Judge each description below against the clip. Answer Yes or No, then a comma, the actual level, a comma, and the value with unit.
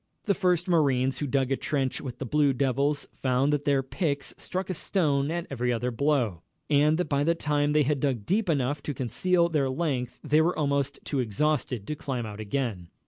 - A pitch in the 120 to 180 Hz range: Yes, medium, 140 Hz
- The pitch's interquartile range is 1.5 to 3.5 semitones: Yes, average, 3.0 semitones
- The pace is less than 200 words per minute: No, fast, 205 wpm